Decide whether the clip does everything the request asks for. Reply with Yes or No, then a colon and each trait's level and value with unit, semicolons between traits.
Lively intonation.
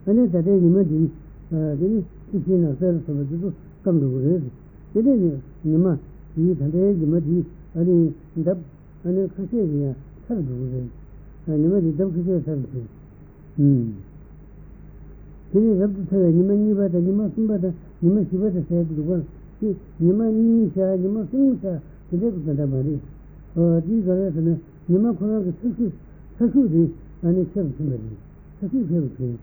No: average, 4.2 semitones